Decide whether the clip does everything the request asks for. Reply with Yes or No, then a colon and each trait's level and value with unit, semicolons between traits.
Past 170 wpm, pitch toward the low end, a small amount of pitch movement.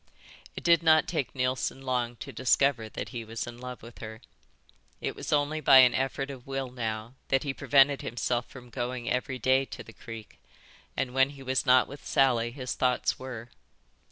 Yes: average, 190 wpm; low, 130 Hz; narrow, 2.1 semitones